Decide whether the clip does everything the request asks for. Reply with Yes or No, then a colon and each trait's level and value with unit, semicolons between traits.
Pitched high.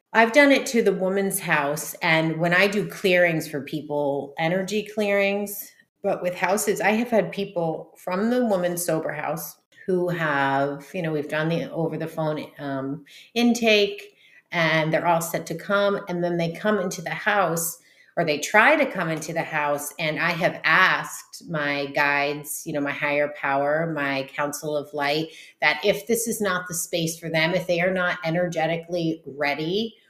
No: medium, 165 Hz